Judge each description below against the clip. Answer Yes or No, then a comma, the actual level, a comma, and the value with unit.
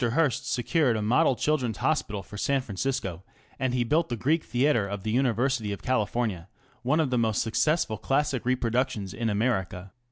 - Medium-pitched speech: No, low, 120 Hz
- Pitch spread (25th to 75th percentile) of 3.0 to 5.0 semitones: Yes, average, 4.1 semitones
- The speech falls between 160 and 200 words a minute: Yes, average, 180 wpm